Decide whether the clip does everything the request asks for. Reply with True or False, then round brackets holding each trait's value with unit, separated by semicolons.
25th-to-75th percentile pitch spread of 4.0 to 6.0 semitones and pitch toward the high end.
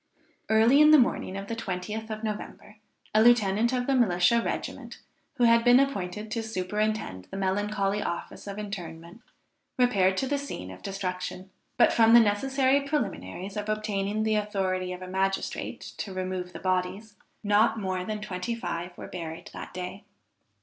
False (3.4 semitones; 205 Hz)